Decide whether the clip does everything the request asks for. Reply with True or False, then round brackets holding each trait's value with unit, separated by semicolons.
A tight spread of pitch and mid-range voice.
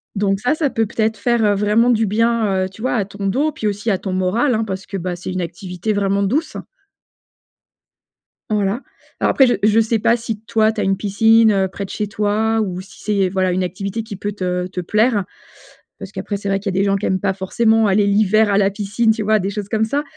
False (2.3 semitones; 205 Hz)